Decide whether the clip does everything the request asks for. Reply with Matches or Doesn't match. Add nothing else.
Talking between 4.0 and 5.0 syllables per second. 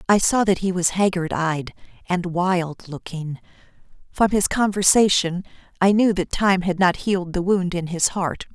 Matches